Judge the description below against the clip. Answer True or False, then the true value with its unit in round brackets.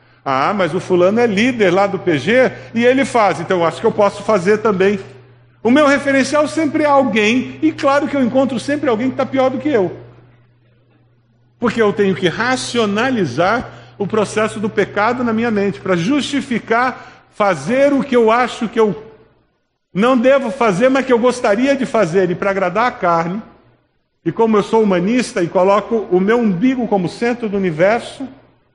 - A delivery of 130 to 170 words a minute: False (185 wpm)